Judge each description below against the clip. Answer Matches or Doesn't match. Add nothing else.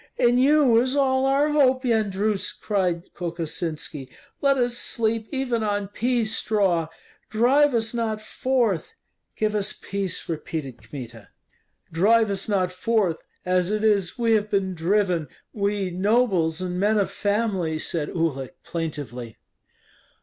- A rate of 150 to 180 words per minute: Doesn't match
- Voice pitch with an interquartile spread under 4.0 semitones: Doesn't match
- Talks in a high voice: Matches